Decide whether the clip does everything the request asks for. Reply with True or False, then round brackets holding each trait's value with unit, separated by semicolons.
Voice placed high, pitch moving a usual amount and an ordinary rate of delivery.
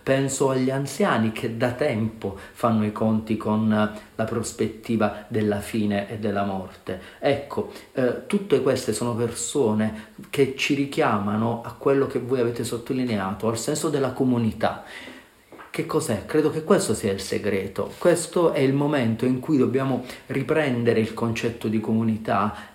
False (115 Hz; 3.7 semitones; 150 wpm)